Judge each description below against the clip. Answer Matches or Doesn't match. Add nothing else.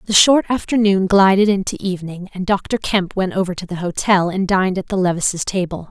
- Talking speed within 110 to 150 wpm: Doesn't match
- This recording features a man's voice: Doesn't match